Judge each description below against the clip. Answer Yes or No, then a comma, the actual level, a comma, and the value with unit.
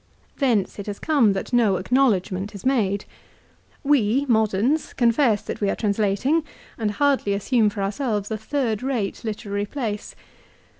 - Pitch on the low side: No, high, 220 Hz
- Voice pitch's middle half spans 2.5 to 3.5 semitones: No, average, 4.4 semitones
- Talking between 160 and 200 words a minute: No, average, 145 wpm